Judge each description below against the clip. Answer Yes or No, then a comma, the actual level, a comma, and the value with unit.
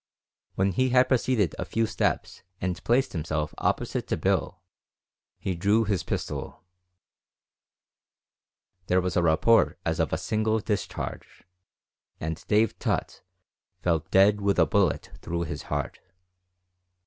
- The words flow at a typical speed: No, slow, 130 wpm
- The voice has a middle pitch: No, very low, 95 Hz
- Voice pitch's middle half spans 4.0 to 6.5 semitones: Yes, average, 4.5 semitones